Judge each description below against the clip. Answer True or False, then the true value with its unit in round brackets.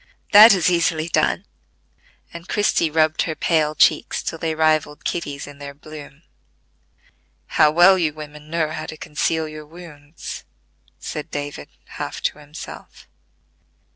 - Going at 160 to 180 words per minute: False (140 wpm)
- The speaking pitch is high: False (155 Hz)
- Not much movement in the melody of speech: True (1.9 semitones)